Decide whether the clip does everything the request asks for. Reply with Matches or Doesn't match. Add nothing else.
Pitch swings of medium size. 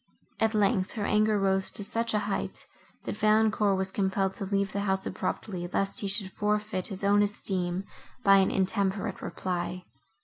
Doesn't match